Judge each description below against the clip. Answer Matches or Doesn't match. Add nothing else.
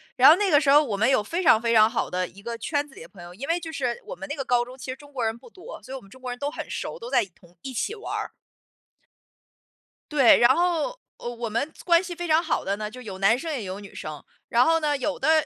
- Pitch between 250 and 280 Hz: Matches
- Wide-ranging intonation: Matches